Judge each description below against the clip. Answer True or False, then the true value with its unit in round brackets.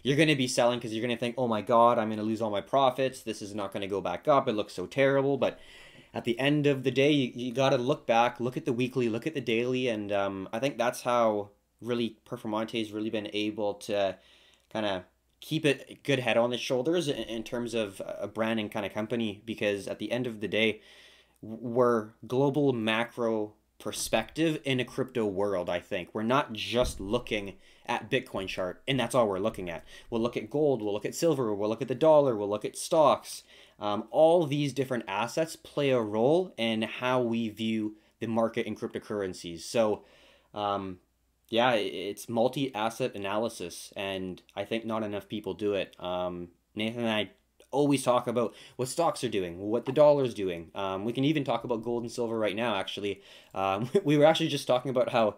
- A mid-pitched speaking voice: False (115 Hz)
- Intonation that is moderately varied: True (3.6 semitones)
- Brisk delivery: True (210 wpm)